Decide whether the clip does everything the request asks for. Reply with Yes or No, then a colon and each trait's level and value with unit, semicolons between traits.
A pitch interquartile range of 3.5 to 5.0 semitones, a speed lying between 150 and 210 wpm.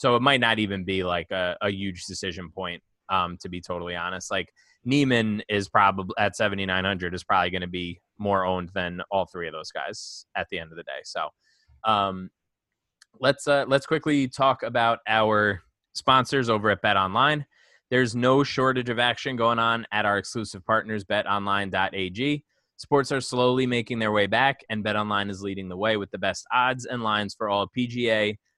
Yes: average, 4.4 semitones; average, 195 wpm